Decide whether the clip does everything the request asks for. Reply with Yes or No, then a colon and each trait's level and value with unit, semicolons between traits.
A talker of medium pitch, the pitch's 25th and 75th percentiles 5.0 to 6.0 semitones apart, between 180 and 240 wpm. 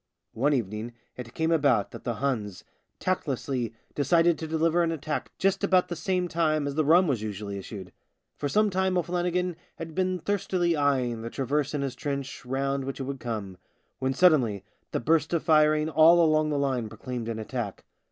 Yes: medium, 145 Hz; wide, 5.4 semitones; average, 190 wpm